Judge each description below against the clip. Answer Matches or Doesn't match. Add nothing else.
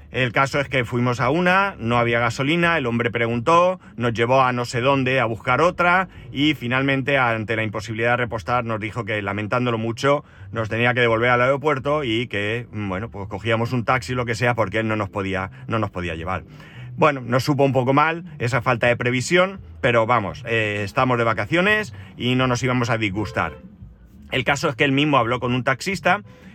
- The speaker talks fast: Matches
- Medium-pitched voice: Doesn't match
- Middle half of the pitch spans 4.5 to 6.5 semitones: Doesn't match